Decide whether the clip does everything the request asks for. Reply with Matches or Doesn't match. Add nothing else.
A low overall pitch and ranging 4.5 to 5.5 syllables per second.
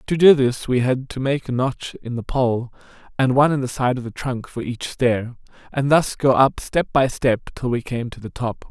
Matches